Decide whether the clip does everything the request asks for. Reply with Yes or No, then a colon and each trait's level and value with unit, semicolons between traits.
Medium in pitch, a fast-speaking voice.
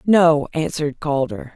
No: medium, 155 Hz; slow, 115 wpm